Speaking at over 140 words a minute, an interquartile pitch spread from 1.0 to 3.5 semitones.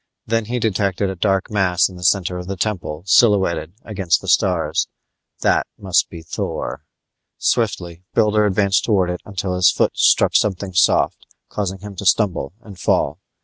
Yes: average, 165 wpm; narrow, 2.6 semitones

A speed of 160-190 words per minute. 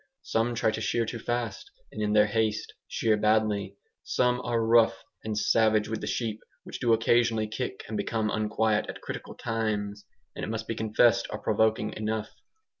Yes: average, 180 wpm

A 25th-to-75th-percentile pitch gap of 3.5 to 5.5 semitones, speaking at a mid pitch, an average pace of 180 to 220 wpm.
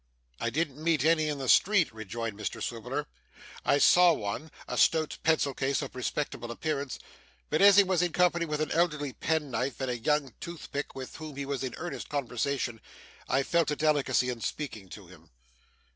Yes: average, 4.0 semitones; medium, 145 Hz; average, 185 wpm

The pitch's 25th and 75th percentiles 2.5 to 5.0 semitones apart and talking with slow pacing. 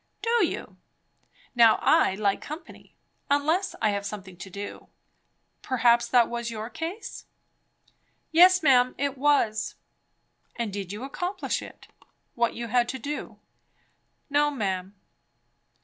No: wide, 5.6 semitones; slow, 130 wpm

